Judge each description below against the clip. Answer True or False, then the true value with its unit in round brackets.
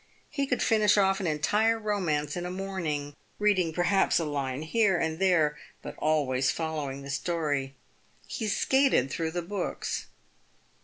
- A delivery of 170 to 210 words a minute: False (150 wpm)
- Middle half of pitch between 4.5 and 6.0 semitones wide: True (5.2 semitones)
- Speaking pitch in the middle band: True (170 Hz)